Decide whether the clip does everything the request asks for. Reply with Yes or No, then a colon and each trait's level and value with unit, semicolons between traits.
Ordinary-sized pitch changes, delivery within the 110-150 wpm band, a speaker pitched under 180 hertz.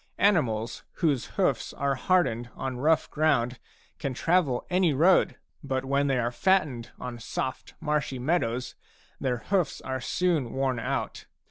Yes: average, 4.7 semitones; average, 140 wpm; low, 135 Hz